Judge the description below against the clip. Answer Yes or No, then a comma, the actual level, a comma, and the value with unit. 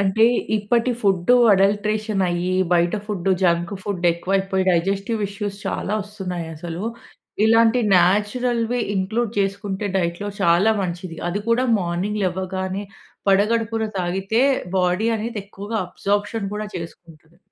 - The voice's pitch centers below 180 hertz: No, high, 195 Hz